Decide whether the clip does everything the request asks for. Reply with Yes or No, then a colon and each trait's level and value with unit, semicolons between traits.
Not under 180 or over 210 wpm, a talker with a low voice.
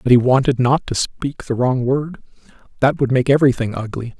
Yes: average, 200 wpm; low, 130 Hz